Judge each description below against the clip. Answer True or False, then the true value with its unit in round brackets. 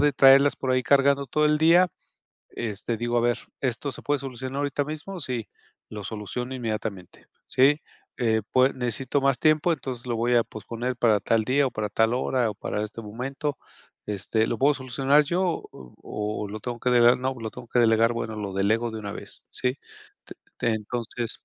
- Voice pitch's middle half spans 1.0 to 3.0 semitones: False (3.6 semitones)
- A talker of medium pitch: False (120 Hz)